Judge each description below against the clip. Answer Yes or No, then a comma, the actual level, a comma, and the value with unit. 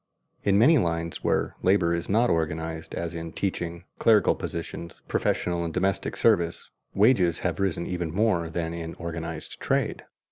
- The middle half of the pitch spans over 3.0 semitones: No, average, 2.7 semitones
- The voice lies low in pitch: Yes, very low, 85 Hz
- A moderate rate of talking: Yes, average, 150 wpm